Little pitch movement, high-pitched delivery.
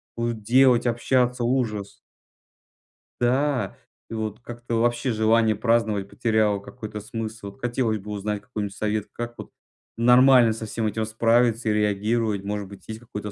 No: narrow, 2.2 semitones; low, 110 Hz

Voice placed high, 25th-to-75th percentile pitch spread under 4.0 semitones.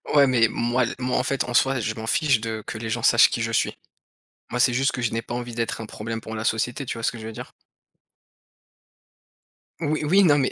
No: low, 120 Hz; average, 2.8 semitones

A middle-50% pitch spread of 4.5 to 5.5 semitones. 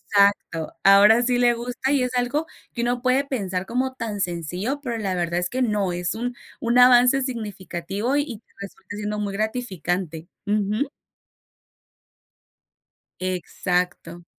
Yes: average, 5.0 semitones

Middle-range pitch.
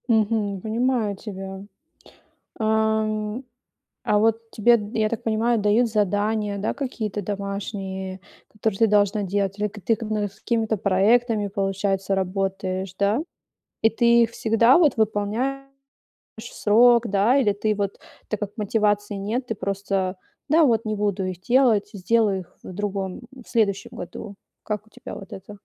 No: high, 210 Hz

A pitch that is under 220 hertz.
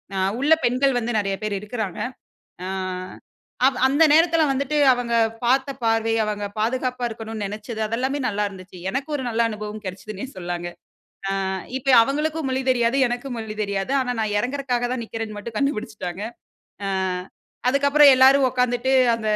No: high, 240 Hz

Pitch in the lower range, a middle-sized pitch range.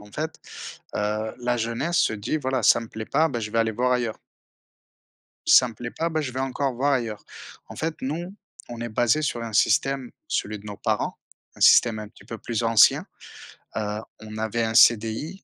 Yes: low, 120 Hz; average, 3.5 semitones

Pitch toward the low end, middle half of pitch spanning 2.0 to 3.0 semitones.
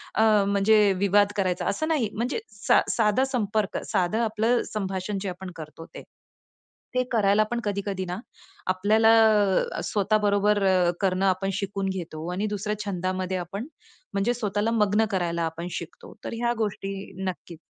No: high, 200 Hz; narrow, 2.5 semitones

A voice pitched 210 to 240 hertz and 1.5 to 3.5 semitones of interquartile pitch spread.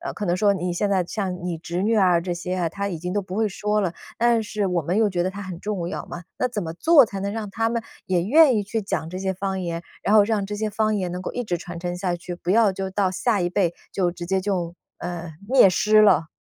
No: high, 190 Hz; average, 3.0 semitones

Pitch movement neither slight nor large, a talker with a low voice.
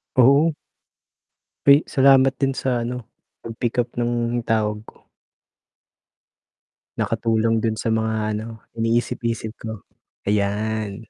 No: narrow, 2.1 semitones; low, 115 Hz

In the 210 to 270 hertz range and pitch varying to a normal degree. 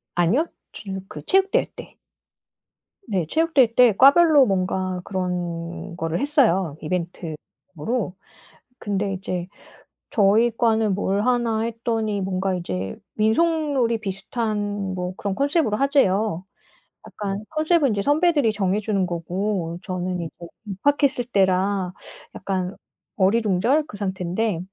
No: high, 200 Hz; average, 4.4 semitones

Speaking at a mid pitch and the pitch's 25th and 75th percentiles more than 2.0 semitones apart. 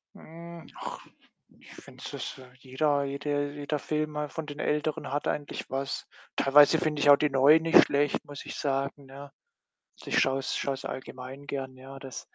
No: medium, 145 Hz; narrow, 1.7 semitones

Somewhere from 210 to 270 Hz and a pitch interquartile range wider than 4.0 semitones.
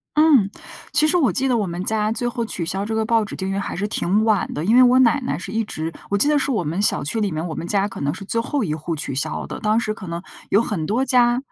Yes: high, 215 Hz; average, 4.6 semitones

